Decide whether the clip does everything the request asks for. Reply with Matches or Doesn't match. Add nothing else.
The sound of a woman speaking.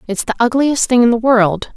Matches